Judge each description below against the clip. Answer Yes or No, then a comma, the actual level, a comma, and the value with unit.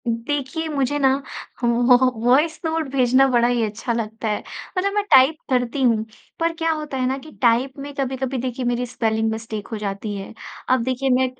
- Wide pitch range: No, average, 3.1 semitones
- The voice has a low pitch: No, very high, 255 Hz